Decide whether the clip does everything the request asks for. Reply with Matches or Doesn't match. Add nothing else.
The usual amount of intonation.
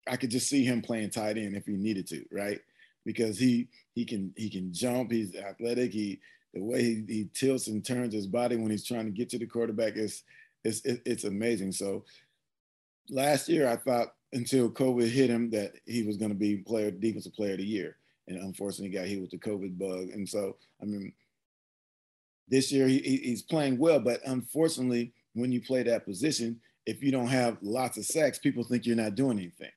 Matches